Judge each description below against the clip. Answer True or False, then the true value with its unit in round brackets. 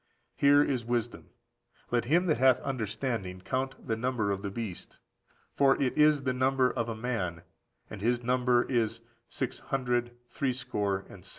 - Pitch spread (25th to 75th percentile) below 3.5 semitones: True (2.9 semitones)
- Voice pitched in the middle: False (120 Hz)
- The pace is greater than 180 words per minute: False (165 wpm)